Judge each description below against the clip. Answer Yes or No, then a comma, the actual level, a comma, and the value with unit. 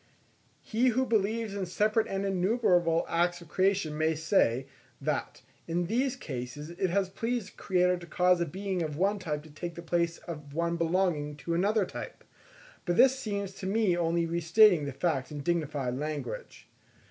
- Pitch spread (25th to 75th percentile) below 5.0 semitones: Yes, average, 3.9 semitones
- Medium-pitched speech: Yes, medium, 175 Hz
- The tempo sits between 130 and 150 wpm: No, average, 175 wpm